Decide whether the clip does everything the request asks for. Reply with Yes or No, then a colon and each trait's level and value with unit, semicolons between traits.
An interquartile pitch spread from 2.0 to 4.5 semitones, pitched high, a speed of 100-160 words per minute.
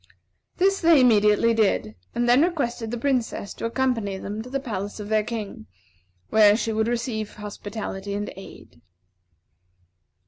Yes: average, 2.8 semitones; high, 220 Hz; average, 145 wpm